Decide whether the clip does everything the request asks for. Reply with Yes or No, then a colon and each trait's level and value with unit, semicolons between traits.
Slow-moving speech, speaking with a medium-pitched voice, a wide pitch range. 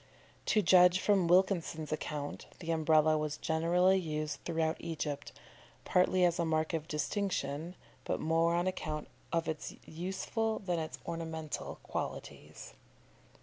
No: slow, 130 wpm; medium, 165 Hz; narrow, 2.5 semitones